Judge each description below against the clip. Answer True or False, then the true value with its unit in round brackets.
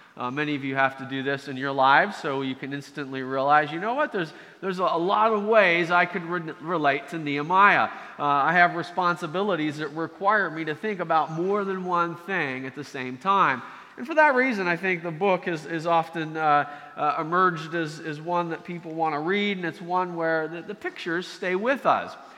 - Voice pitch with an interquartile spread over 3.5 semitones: True (3.9 semitones)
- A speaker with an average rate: False (220 wpm)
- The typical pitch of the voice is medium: True (165 Hz)